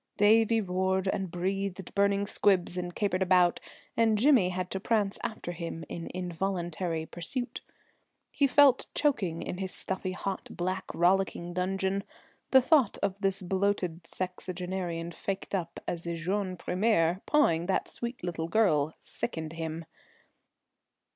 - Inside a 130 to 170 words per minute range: Yes, slow, 135 wpm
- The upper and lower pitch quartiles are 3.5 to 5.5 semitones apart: No, narrow, 2.5 semitones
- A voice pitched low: No, medium, 185 Hz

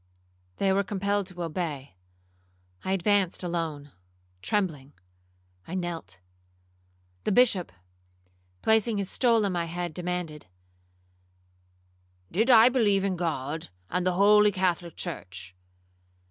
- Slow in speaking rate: Yes, slow, 110 wpm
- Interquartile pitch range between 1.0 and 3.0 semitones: No, average, 3.6 semitones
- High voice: No, medium, 180 Hz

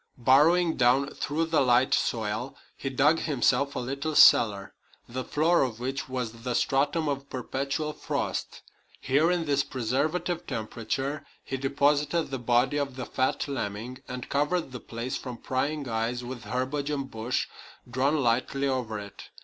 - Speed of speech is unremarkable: Yes, average, 155 wpm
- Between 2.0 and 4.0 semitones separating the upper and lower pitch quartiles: Yes, average, 3.0 semitones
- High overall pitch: No, low, 135 Hz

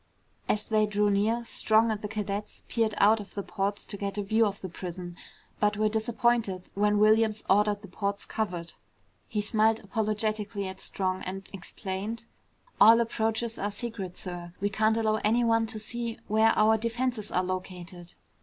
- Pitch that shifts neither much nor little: No, narrow, 2.0 semitones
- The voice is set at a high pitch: Yes, high, 210 Hz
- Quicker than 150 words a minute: Yes, average, 170 wpm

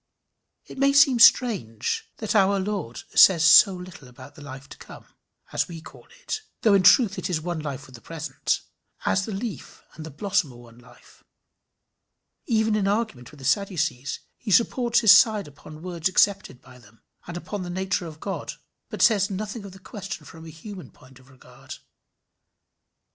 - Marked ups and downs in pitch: Yes, wide, 6.1 semitones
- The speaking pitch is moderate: Yes, medium, 180 Hz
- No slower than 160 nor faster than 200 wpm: Yes, average, 185 wpm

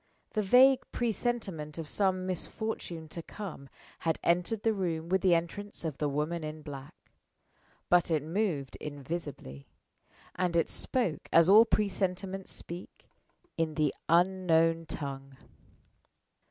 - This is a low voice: No, medium, 170 Hz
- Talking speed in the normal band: No, slow, 125 wpm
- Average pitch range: Yes, average, 3.9 semitones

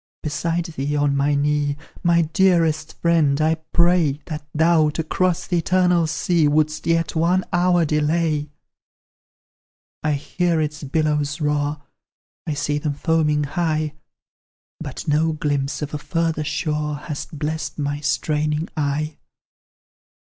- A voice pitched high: No, medium, 155 Hz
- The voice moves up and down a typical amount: No, narrow, 2.0 semitones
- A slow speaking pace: Yes, slow, 130 wpm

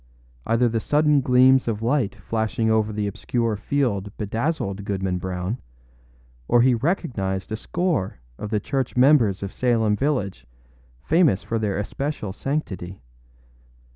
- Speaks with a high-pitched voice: No, low, 110 Hz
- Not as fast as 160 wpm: Yes, slow, 135 wpm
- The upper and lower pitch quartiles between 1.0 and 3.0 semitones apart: No, average, 4.7 semitones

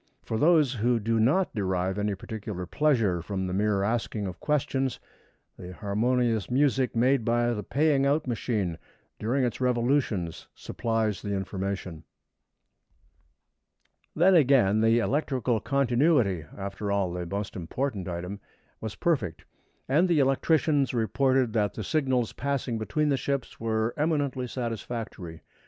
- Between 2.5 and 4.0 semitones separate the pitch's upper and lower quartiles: No, average, 5.2 semitones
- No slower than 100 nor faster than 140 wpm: Yes, slow, 135 wpm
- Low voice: Yes, low, 115 Hz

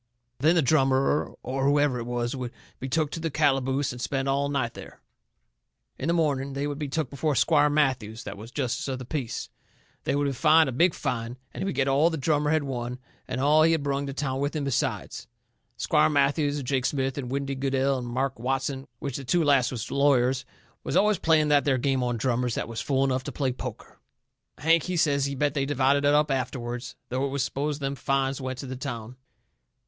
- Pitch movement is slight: Yes, narrow, 2.2 semitones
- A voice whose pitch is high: No, low, 135 Hz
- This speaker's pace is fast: Yes, fast, 225 wpm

